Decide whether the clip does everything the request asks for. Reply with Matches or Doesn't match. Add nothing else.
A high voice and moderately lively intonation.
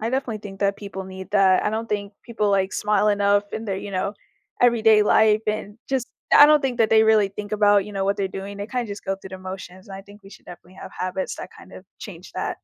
Doesn't match